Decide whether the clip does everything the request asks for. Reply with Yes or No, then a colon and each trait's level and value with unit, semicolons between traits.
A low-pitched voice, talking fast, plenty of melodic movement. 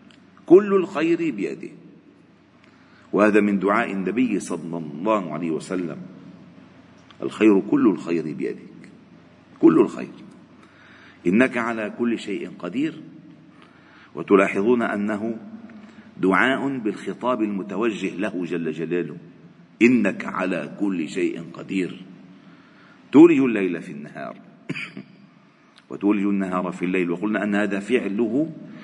No: low, 105 Hz; average, 100 wpm; wide, 5.8 semitones